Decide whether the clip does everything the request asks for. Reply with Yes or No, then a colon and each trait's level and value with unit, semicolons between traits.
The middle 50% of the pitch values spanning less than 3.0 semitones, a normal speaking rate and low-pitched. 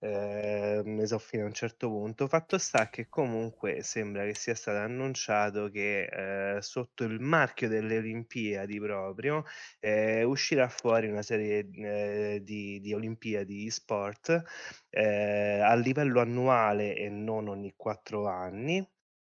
Yes: narrow, 2.5 semitones; average, 140 wpm; low, 110 Hz